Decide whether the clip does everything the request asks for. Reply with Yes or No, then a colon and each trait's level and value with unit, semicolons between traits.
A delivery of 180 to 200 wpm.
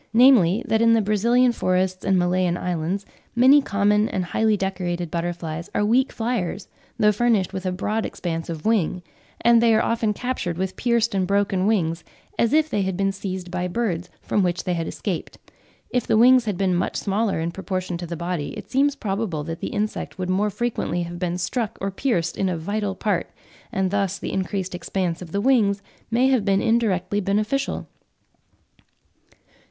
Yes: average, 185 wpm